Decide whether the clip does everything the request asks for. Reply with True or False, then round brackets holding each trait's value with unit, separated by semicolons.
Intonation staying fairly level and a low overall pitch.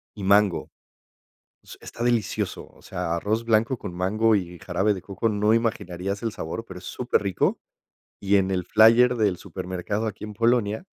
False (3.3 semitones; 105 Hz)